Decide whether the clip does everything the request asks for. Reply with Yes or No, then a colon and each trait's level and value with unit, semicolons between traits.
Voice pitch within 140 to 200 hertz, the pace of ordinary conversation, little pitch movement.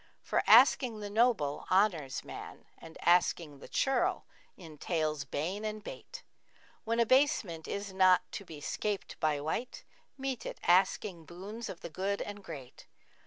No: high, 190 Hz; average, 155 wpm; average, 5.1 semitones